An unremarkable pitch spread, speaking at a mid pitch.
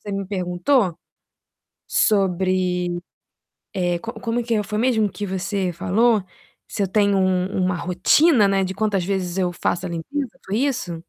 No: average, 3.0 semitones; high, 195 Hz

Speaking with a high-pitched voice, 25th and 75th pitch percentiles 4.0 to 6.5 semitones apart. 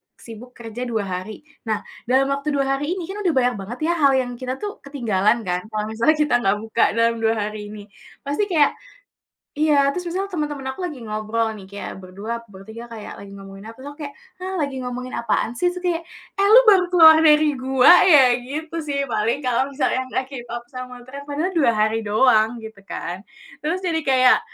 Yes: very high, 255 Hz; average, 5.2 semitones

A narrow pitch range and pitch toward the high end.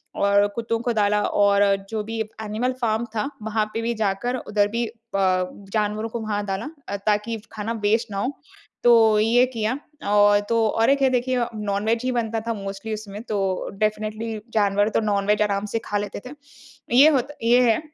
Yes: narrow, 2.0 semitones; high, 215 Hz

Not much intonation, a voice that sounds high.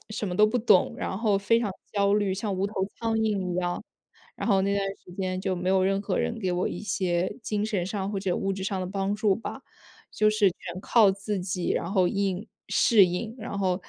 Yes: narrow, 2.3 semitones; high, 195 Hz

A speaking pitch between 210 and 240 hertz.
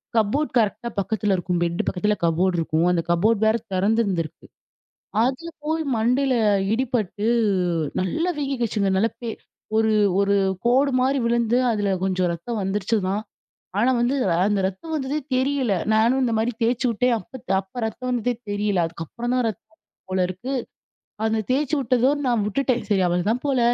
Yes: high, 220 Hz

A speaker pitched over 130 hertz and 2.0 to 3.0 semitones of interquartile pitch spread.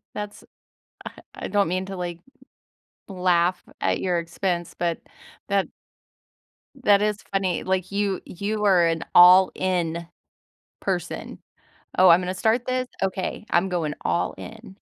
Yes: medium, 185 Hz; narrow, 2.5 semitones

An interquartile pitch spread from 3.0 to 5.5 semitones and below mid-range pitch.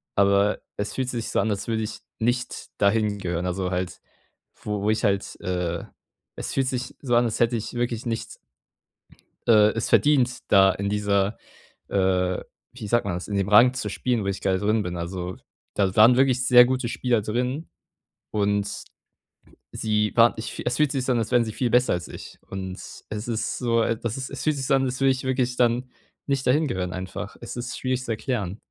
Yes: average, 3.9 semitones; low, 110 Hz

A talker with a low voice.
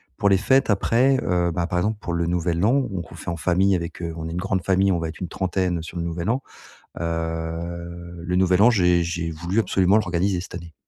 Yes: very low, 90 Hz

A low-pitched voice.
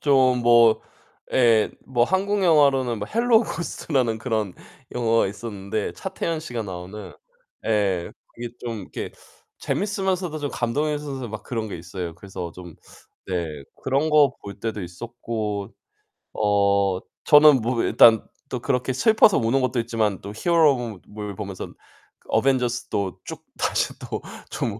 Yes: low, 115 Hz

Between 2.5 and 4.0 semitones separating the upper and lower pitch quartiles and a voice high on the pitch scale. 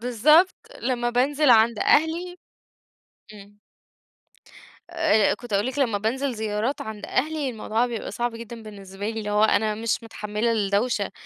Yes: average, 3.6 semitones; high, 230 Hz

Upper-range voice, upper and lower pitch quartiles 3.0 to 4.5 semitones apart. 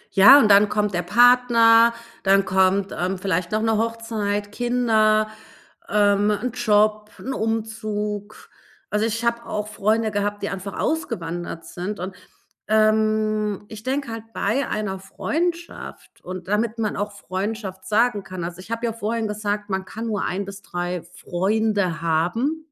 No: high, 210 Hz; narrow, 2.5 semitones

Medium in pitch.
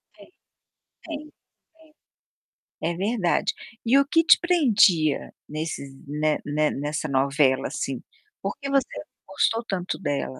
Yes: medium, 175 Hz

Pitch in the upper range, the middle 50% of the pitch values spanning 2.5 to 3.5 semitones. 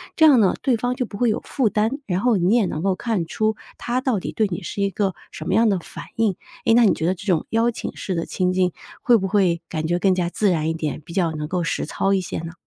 No: high, 195 Hz; average, 4.3 semitones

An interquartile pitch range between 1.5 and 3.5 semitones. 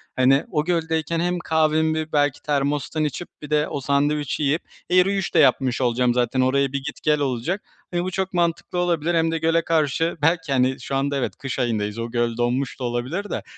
No: average, 4.0 semitones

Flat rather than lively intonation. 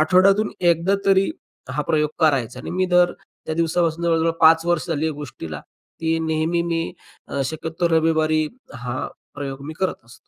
Yes: narrow, 1.7 semitones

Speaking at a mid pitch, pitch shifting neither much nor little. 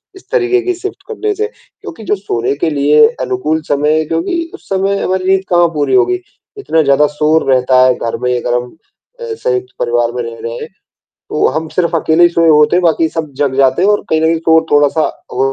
No: medium, 160 Hz; wide, 6.2 semitones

